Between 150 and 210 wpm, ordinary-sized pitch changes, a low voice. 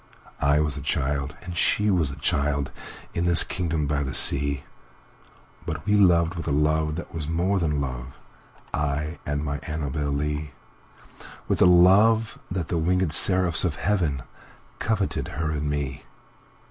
No: average, 140 wpm; average, 3.4 semitones; very low, 75 Hz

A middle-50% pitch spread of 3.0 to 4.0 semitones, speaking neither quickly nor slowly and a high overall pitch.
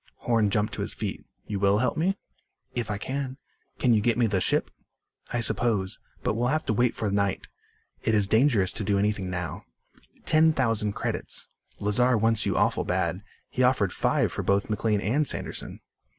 No: average, 3.5 semitones; average, 185 wpm; low, 110 Hz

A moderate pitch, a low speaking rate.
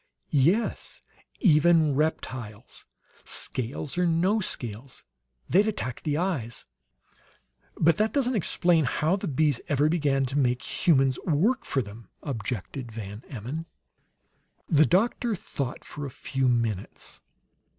Yes: medium, 145 Hz; slow, 120 wpm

